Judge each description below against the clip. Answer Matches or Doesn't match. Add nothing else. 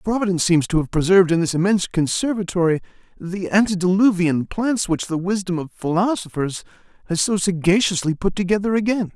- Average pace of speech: Matches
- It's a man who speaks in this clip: Matches